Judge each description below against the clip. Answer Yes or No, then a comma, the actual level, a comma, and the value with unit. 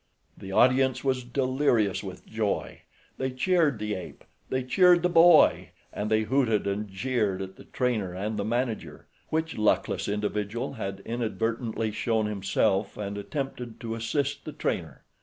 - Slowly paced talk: No, average, 150 wpm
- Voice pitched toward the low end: Yes, low, 115 Hz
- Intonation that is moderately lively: Yes, average, 4.1 semitones